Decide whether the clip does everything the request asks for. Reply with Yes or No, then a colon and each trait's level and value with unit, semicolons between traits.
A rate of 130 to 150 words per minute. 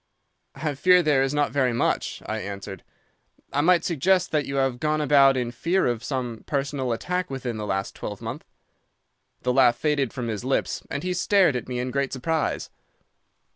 No: average, 185 wpm